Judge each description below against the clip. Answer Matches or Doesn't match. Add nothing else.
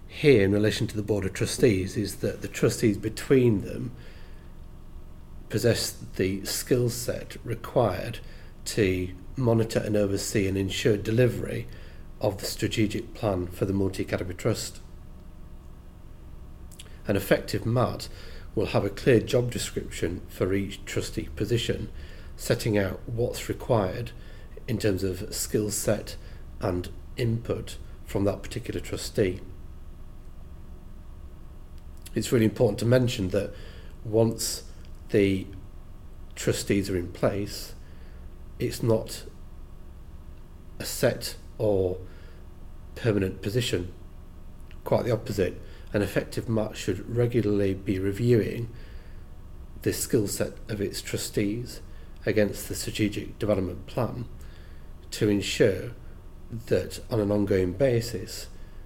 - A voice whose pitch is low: Matches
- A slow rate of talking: Matches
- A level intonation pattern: Doesn't match